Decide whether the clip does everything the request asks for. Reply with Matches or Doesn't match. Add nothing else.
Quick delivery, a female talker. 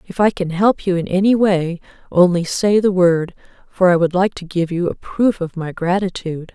Matches